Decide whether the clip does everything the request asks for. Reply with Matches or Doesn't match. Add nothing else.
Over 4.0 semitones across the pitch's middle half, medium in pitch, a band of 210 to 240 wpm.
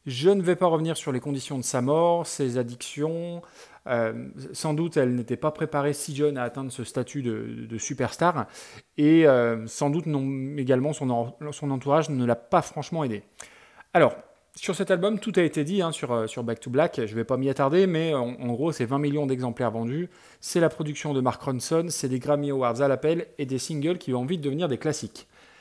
Matches